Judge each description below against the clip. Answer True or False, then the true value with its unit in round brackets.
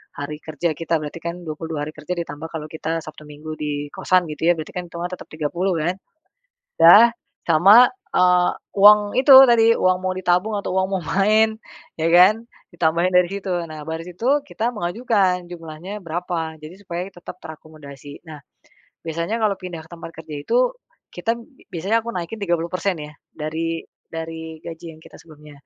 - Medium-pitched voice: True (170 Hz)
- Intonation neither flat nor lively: True (3.2 semitones)